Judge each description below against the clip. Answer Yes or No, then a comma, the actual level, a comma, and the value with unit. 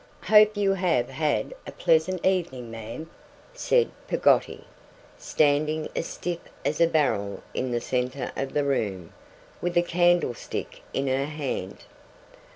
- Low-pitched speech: No, medium, 150 Hz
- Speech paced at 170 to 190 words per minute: No, slow, 135 wpm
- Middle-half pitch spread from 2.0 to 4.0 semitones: No, wide, 5.6 semitones